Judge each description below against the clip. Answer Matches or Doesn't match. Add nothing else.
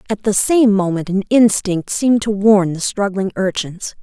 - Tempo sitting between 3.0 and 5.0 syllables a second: Matches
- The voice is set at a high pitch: Matches